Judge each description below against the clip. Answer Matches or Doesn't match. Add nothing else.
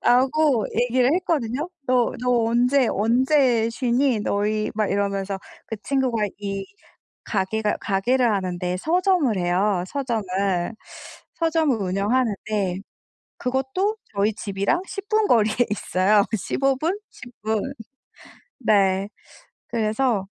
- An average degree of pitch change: Matches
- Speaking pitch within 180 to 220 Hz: Doesn't match